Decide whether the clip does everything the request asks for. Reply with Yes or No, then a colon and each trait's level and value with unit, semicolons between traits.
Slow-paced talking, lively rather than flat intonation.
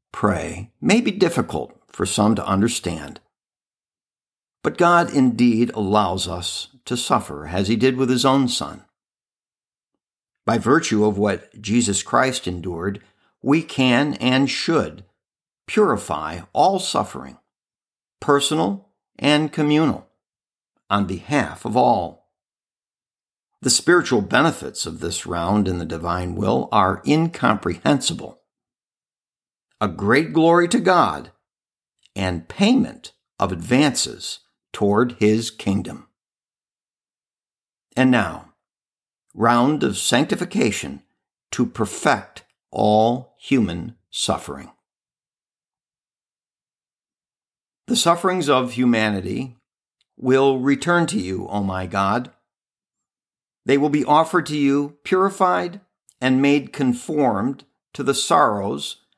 Yes: slow, 100 wpm; wide, 6.3 semitones